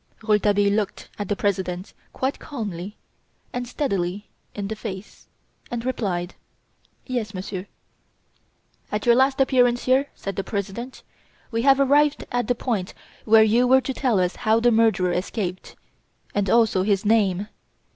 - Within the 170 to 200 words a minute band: No, average, 145 wpm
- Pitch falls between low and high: No, high, 215 Hz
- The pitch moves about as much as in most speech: Yes, average, 4.0 semitones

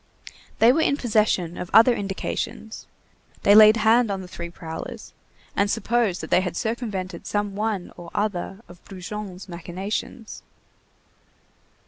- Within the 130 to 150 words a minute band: Yes, slow, 135 wpm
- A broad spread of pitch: No, average, 3.4 semitones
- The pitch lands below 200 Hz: No, high, 205 Hz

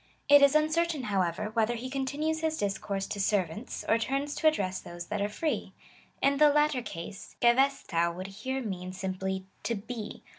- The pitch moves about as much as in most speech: No, wide, 6.6 semitones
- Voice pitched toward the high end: Yes, high, 225 Hz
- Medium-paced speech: Yes, average, 180 wpm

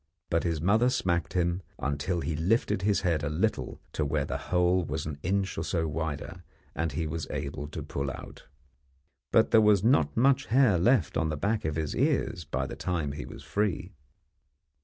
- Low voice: Yes, very low, 85 Hz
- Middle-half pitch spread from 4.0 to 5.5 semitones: Yes, average, 4.7 semitones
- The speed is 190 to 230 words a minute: Yes, average, 195 wpm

